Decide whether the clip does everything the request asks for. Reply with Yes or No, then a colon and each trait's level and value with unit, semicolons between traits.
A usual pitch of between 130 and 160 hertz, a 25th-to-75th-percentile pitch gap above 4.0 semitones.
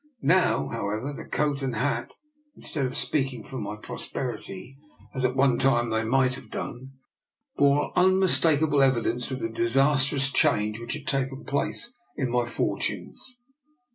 No: low, 135 Hz; average, 3.1 semitones